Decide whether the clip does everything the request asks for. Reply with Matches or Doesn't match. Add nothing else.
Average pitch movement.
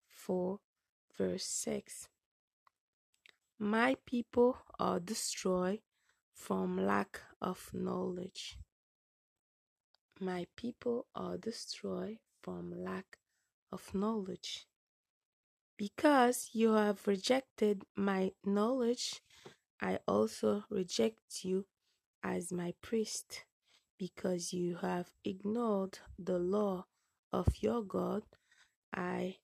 Matches